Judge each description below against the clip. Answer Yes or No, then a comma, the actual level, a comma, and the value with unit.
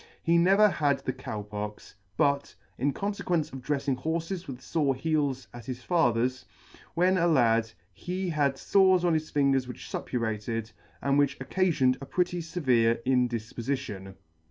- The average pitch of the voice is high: No, medium, 140 Hz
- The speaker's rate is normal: Yes, average, 155 wpm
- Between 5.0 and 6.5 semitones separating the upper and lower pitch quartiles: Yes, wide, 5.4 semitones